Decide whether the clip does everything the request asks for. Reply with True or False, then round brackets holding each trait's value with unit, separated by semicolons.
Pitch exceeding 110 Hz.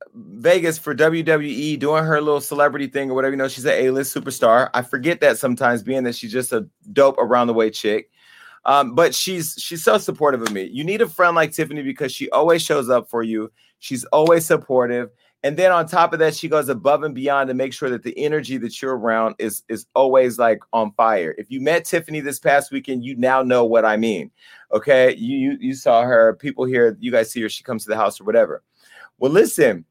True (140 Hz)